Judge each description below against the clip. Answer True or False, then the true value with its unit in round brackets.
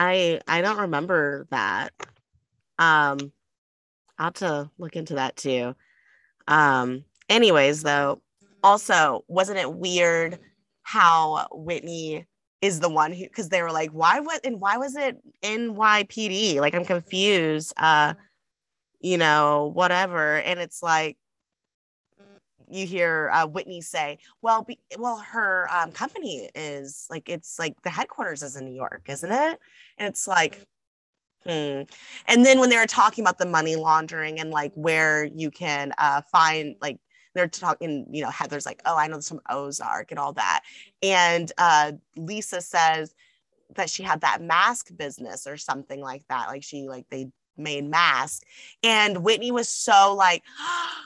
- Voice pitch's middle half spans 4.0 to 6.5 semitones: True (4.7 semitones)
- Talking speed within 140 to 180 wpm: True (155 wpm)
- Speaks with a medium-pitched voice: True (170 Hz)